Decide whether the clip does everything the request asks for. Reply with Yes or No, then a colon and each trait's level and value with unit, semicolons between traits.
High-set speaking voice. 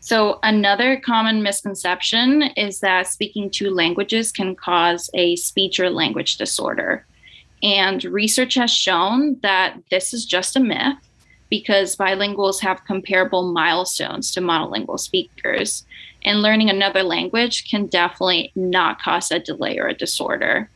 Yes: high, 200 Hz